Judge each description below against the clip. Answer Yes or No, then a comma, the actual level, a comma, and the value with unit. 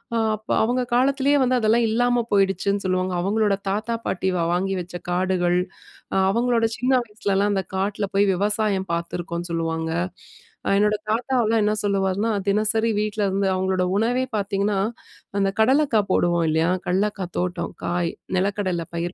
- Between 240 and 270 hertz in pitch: No, high, 200 Hz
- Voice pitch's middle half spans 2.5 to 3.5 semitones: Yes, average, 3.1 semitones